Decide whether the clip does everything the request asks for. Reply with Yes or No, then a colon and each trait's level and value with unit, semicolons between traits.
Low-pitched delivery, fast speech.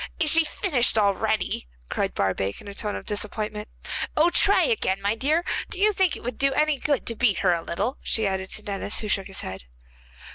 No: high, 215 Hz; fast, 215 wpm